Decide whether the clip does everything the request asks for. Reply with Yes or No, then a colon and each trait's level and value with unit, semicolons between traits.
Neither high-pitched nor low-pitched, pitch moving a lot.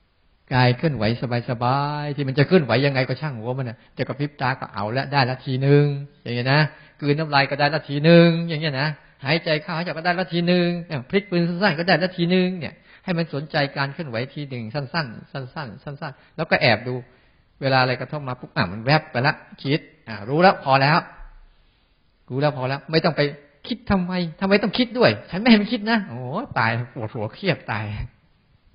No: medium, 145 Hz; average, 4.8 semitones